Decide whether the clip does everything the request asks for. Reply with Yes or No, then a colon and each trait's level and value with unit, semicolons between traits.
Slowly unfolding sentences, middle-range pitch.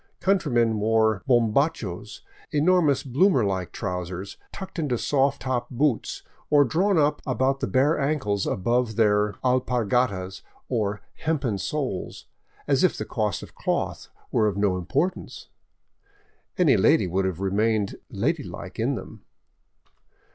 No: slow, 125 wpm; low, 120 Hz